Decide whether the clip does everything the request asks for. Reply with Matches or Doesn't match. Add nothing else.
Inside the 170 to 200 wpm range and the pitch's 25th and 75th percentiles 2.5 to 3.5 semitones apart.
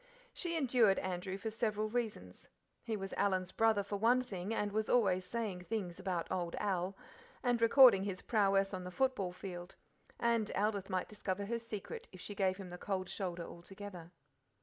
Matches